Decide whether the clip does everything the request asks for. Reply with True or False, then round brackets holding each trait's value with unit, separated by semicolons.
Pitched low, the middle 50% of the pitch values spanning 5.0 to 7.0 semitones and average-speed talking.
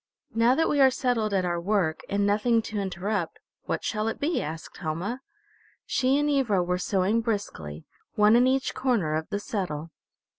False (210 Hz; 5.3 semitones; 180 wpm)